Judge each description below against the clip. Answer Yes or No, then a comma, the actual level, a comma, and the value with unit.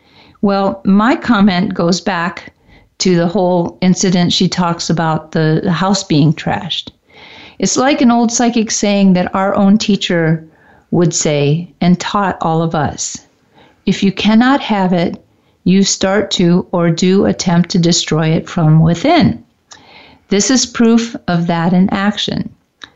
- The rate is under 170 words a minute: Yes, average, 145 wpm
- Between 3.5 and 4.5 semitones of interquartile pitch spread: No, average, 3.1 semitones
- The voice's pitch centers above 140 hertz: Yes, medium, 185 Hz